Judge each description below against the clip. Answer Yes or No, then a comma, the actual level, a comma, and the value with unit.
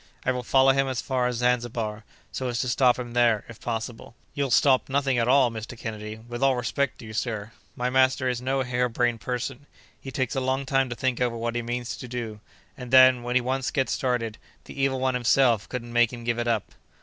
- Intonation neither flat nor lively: No, narrow, 1.8 semitones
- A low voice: Yes, low, 125 Hz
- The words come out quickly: Yes, fast, 235 wpm